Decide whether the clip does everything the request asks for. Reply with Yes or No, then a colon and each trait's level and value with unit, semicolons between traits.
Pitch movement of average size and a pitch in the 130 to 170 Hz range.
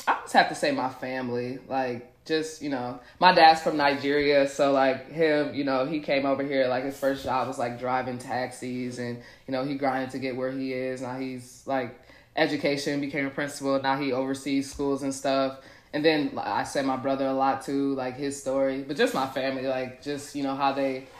No: narrow, 1.5 semitones; low, 135 Hz